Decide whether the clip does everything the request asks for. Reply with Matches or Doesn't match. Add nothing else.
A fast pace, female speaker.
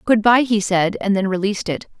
Matches